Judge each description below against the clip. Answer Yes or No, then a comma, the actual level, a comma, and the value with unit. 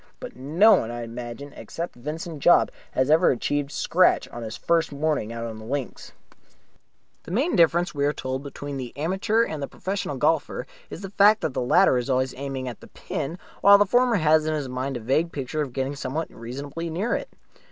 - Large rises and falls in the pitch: No, average, 4.6 semitones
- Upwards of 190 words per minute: Yes, fast, 205 wpm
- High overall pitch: No, medium, 145 Hz